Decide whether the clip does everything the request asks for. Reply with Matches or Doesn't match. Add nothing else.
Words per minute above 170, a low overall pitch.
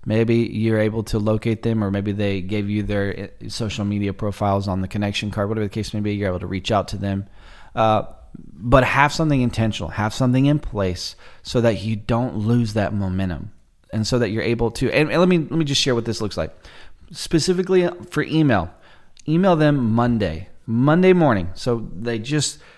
Matches